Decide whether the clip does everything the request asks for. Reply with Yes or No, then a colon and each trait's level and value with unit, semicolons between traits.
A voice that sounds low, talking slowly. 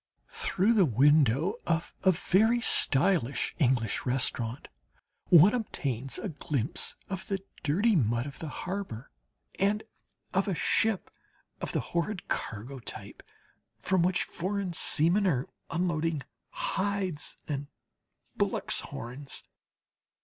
No: medium, 165 Hz; slow, 115 wpm